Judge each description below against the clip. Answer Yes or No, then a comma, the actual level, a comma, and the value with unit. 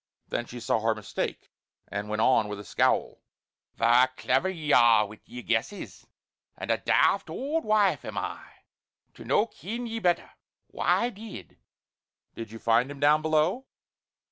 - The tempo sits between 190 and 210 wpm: No, average, 165 wpm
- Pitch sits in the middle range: No, low, 130 Hz